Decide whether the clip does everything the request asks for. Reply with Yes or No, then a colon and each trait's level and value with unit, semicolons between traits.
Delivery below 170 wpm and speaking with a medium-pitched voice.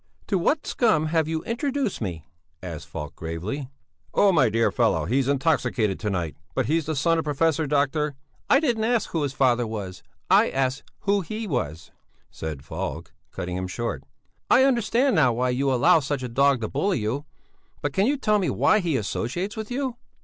No: average, 190 wpm; medium, 145 Hz